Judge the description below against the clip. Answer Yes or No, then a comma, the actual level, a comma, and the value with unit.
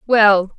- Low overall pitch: No, high, 210 Hz